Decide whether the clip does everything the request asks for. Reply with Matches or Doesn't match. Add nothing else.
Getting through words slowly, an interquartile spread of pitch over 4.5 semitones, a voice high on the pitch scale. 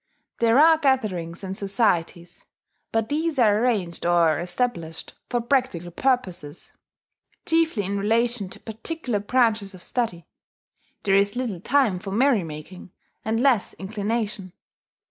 Matches